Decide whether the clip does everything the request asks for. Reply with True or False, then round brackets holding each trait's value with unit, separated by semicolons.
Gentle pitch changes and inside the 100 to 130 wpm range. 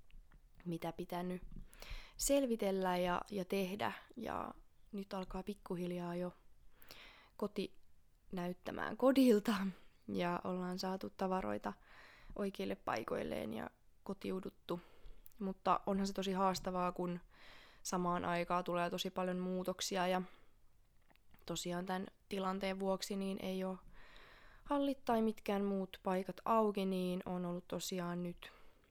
True (1.7 semitones; 105 wpm)